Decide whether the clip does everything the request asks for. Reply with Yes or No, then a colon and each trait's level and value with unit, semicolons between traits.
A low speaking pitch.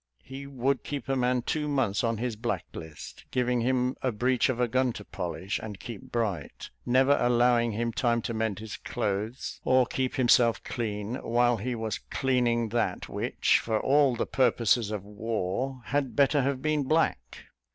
Yes: low, 120 Hz